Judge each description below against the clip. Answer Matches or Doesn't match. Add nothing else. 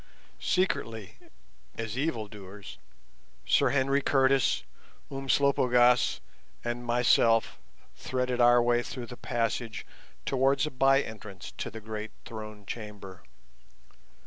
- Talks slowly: Matches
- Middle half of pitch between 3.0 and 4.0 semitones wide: Matches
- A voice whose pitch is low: Matches